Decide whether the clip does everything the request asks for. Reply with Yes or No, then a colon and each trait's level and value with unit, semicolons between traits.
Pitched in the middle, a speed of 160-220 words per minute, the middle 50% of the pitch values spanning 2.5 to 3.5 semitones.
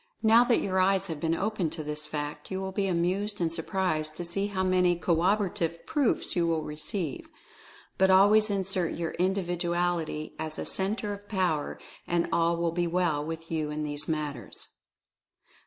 Yes: medium, 175 Hz; average, 170 wpm; average, 3.1 semitones